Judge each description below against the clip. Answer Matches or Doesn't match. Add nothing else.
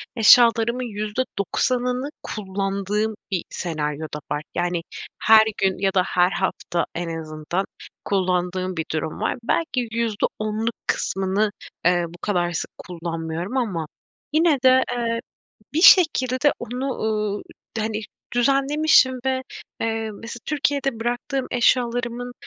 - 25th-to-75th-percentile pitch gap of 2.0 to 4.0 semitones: Doesn't match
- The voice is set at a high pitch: Matches